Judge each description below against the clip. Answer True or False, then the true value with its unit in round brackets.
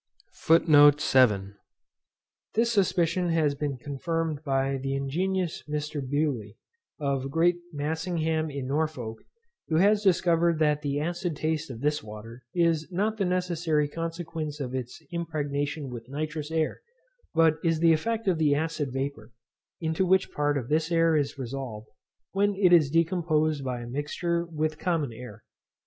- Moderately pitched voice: True (155 Hz)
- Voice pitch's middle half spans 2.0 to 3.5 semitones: True (3.2 semitones)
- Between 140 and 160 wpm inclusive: True (145 wpm)